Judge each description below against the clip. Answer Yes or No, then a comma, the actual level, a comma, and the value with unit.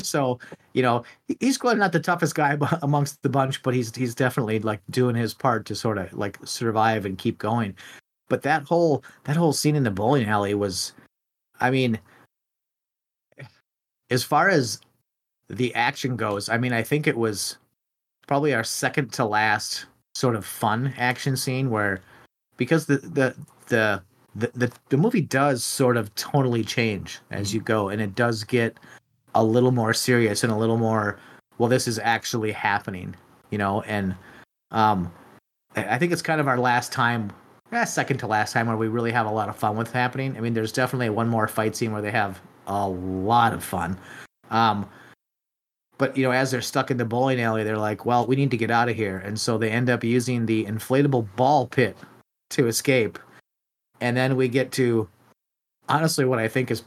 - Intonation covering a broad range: No, average, 3.3 semitones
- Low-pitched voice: Yes, low, 120 Hz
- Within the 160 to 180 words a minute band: No, average, 190 wpm